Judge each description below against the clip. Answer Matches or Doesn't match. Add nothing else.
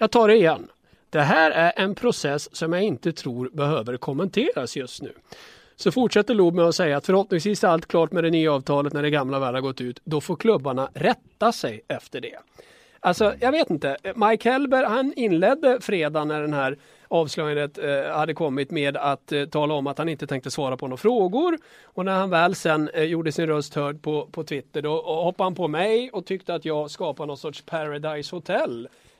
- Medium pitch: Matches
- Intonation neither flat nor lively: Matches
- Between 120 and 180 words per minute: Doesn't match